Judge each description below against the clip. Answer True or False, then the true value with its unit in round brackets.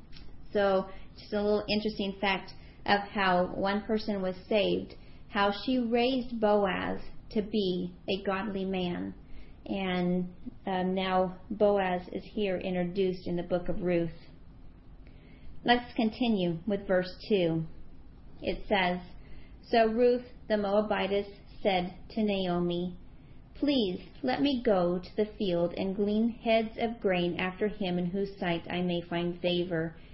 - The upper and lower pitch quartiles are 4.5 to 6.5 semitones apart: False (3.0 semitones)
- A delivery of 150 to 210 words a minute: False (135 wpm)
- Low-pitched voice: False (195 Hz)